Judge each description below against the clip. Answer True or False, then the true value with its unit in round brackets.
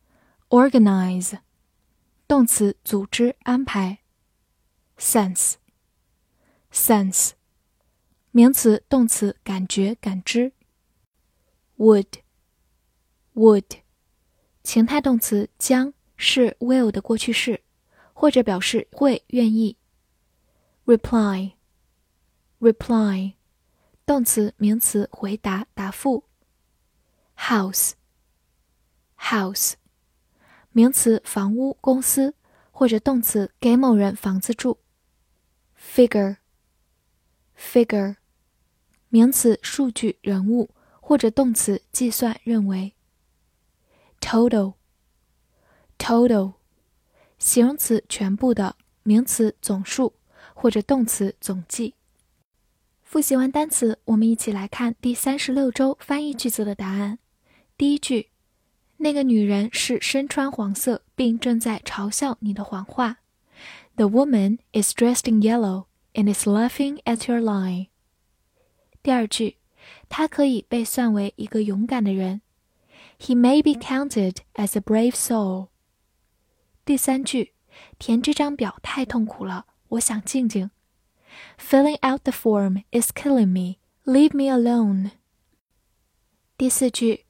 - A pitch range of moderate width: True (4.1 semitones)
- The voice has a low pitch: False (225 Hz)